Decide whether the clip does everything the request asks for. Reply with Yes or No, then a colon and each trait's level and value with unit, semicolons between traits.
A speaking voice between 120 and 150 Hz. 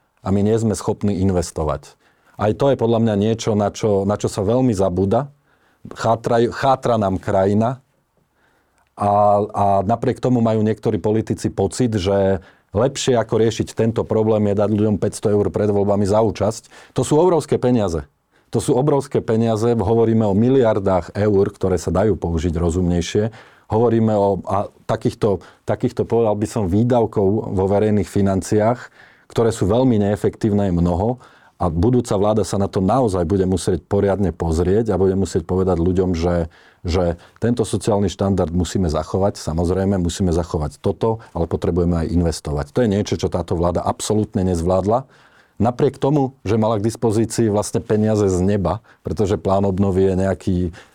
No: low, 100 Hz